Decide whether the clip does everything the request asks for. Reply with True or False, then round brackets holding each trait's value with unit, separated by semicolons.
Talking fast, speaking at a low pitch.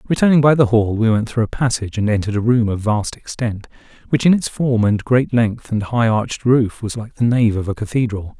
True (245 wpm; 115 Hz)